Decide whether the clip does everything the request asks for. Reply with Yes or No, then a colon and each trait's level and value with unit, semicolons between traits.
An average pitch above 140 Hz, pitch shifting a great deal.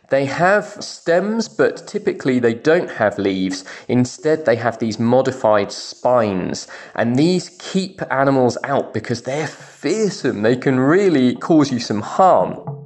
No: low, 135 Hz; wide, 6.4 semitones